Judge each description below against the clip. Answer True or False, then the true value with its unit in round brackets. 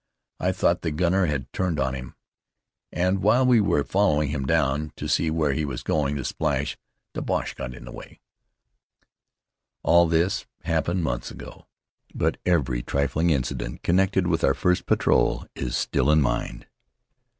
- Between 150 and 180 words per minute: True (160 wpm)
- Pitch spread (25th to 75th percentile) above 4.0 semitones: True (4.8 semitones)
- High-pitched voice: False (80 Hz)